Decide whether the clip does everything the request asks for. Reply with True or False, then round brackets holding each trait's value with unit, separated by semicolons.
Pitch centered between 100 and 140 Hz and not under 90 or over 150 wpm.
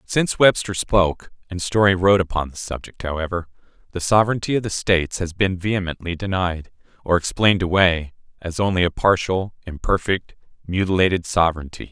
False (90 Hz; 145 wpm)